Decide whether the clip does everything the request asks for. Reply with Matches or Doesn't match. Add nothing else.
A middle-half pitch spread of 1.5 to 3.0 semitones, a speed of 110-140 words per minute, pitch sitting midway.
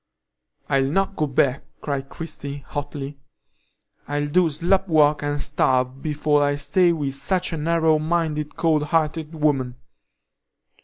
Matches